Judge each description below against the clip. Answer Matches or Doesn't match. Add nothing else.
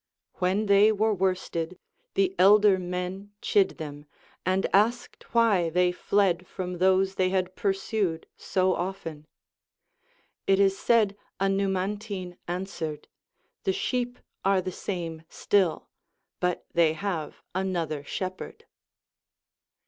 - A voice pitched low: Doesn't match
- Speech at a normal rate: Doesn't match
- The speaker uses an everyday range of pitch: Doesn't match